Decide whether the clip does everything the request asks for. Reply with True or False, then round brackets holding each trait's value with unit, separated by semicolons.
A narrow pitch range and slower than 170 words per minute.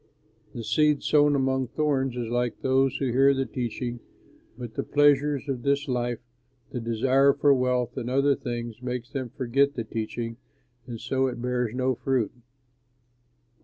True (2.3 semitones; 160 wpm)